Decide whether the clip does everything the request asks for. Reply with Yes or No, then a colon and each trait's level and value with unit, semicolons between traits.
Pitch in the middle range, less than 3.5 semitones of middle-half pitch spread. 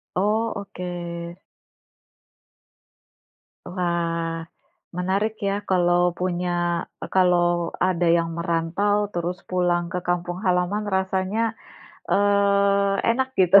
Yes: medium, 180 Hz; narrow, 2.4 semitones